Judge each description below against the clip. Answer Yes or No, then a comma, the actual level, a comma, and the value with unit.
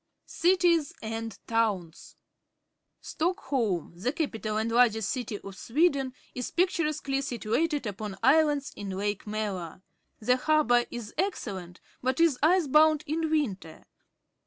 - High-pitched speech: Yes, very high, 250 Hz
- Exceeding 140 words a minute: No, slow, 135 wpm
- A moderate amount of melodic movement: No, wide, 6.6 semitones